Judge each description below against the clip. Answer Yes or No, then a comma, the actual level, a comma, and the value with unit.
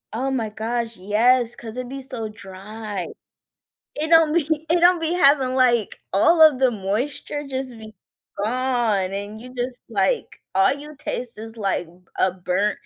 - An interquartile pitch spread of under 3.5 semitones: No, average, 4.3 semitones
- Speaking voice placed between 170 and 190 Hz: No, high, 240 Hz